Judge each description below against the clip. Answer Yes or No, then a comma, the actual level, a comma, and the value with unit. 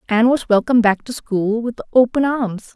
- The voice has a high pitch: Yes, high, 235 Hz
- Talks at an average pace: Yes, average, 195 wpm